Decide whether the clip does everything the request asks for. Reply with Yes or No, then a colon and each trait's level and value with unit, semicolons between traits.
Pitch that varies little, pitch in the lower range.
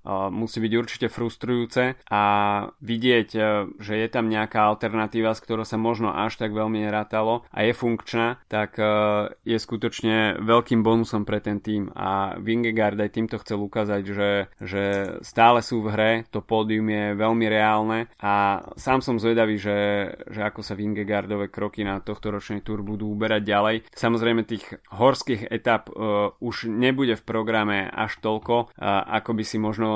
Yes: narrow, 1.6 semitones; low, 110 Hz